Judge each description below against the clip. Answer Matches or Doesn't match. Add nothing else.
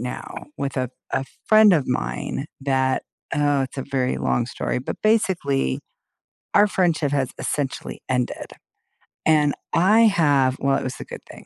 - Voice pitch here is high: Doesn't match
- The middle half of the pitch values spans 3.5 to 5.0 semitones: Matches